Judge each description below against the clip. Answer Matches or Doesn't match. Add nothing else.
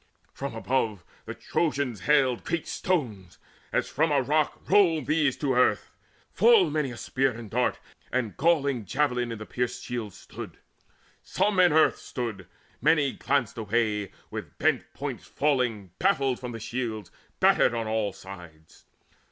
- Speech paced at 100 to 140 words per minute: Doesn't match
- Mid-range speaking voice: Doesn't match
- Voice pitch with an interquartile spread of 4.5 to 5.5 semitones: Matches